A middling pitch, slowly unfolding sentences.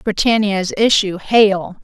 No: high, 200 Hz; slow, 100 wpm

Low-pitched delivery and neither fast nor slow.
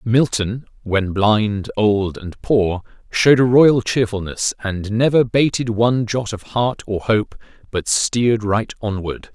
Yes: low, 110 Hz; average, 150 wpm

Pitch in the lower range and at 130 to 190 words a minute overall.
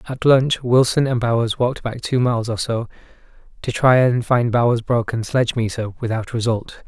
Yes: low, 120 Hz; average, 175 wpm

